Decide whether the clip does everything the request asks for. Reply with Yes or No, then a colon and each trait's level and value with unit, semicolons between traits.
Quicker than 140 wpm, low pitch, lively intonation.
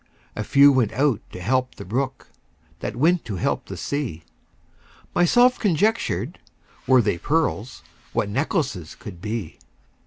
No: slow, 135 wpm; low, 130 Hz; wide, 6.7 semitones